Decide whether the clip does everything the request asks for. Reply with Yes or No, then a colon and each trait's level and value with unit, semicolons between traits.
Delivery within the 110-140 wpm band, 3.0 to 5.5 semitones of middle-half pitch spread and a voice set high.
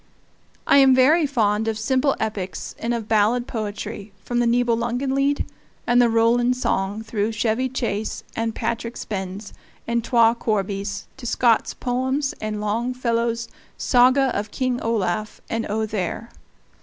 No: slow, 135 wpm; narrow, 2.5 semitones; high, 230 Hz